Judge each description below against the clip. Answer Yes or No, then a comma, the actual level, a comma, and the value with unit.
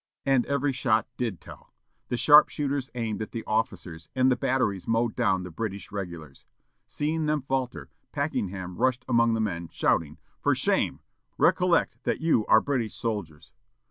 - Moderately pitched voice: No, low, 115 Hz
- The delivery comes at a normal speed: Yes, average, 155 wpm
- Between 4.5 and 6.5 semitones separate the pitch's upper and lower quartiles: Yes, wide, 5.6 semitones